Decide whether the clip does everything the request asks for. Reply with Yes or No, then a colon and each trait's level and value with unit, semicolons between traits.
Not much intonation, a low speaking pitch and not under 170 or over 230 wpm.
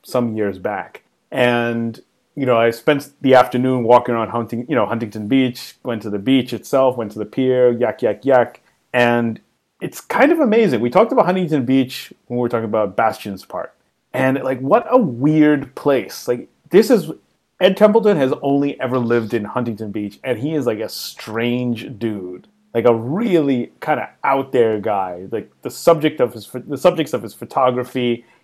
No: average, 3.2 semitones; low, 125 Hz; average, 190 wpm